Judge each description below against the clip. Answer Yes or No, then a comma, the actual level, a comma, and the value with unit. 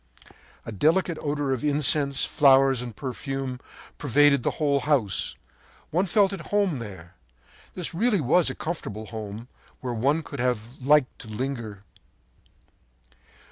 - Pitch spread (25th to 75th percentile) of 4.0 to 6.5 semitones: Yes, average, 4.3 semitones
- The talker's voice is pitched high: No, low, 135 Hz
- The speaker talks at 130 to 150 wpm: Yes, slow, 135 wpm